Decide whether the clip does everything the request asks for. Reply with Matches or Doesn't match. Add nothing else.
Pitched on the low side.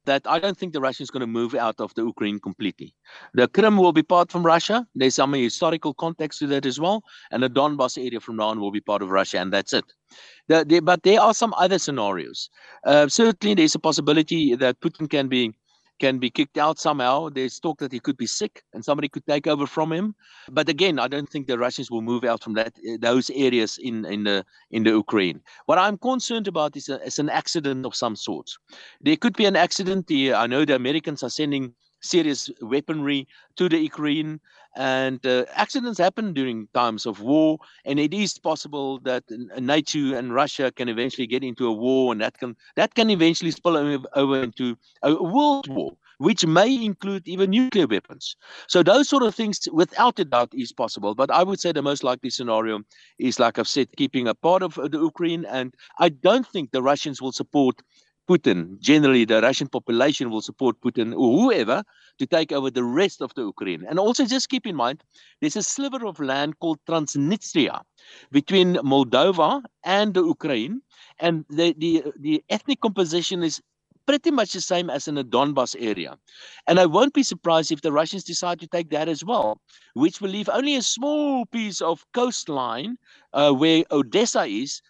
Doesn't match